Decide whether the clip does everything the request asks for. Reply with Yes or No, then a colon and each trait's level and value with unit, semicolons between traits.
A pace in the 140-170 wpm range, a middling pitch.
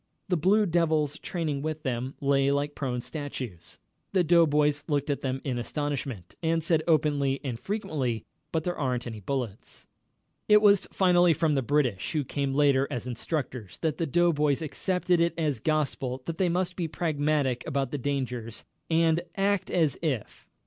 Yes: average, 165 wpm; medium, 145 Hz